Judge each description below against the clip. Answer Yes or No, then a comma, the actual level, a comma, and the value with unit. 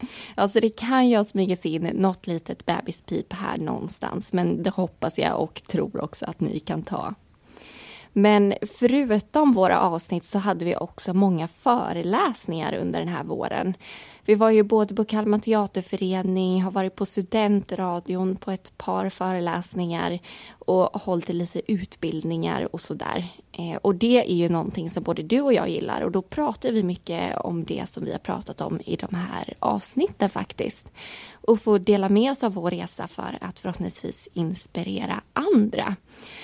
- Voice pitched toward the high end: Yes, high, 195 Hz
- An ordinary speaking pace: Yes, average, 165 wpm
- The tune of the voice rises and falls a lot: No, average, 3.4 semitones